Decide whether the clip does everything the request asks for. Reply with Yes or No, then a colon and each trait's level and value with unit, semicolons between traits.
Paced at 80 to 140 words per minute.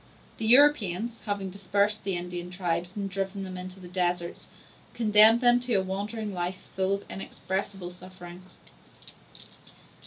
Yes: slow, 135 wpm